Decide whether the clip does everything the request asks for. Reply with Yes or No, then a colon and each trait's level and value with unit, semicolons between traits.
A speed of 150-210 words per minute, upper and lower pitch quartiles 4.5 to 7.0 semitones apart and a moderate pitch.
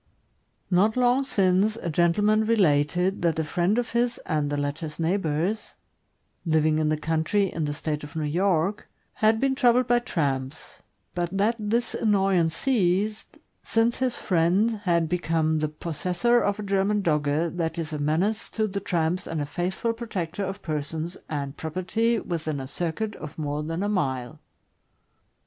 Yes: average, 165 wpm; average, 5.1 semitones; medium, 175 Hz